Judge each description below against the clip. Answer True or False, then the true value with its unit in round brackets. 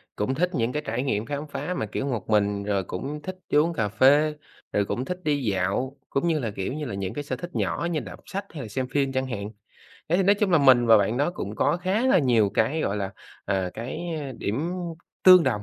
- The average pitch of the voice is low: True (130 Hz)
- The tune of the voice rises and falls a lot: True (6.7 semitones)